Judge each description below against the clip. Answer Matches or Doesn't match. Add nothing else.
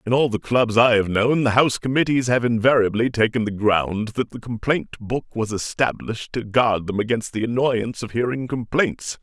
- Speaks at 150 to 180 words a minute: Doesn't match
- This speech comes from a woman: Doesn't match